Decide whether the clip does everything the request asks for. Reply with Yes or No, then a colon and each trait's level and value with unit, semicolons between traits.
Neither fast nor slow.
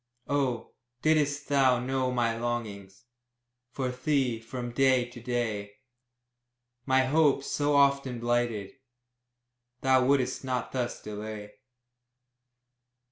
No: slow, 100 wpm